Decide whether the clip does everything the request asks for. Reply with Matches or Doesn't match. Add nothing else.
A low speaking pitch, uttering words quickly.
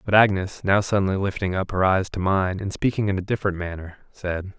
Matches